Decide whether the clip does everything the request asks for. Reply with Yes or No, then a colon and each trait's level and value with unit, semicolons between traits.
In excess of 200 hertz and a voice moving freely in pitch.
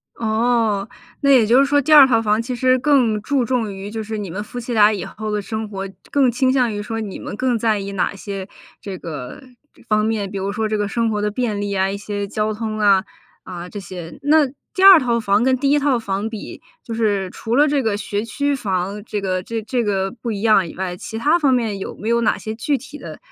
No: high, 220 Hz; average, 3.5 semitones